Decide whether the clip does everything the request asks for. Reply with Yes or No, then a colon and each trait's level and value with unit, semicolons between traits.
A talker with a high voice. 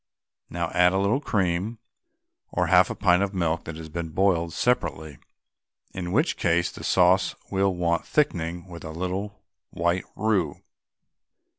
No: very low, 90 Hz